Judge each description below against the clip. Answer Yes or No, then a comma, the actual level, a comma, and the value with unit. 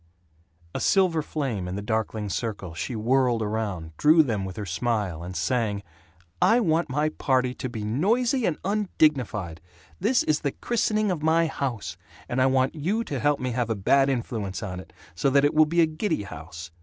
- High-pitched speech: No, low, 130 Hz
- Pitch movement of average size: No, wide, 7.2 semitones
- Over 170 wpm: Yes, average, 195 wpm